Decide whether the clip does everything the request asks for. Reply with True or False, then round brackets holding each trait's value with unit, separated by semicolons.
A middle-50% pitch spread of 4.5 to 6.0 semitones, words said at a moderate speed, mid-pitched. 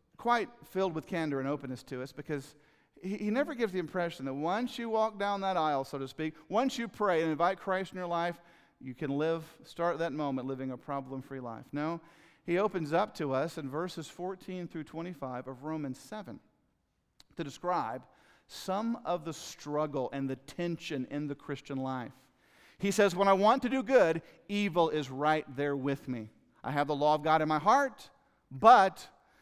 True (4.8 semitones; 195 wpm; 160 Hz)